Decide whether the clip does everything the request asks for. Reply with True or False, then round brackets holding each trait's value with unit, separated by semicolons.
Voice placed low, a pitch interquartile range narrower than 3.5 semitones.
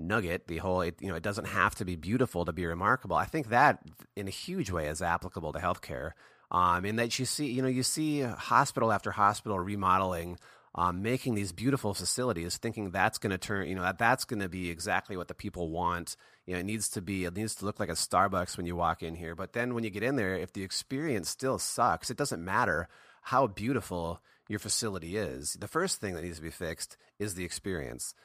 False (95 Hz; 4.0 semitones)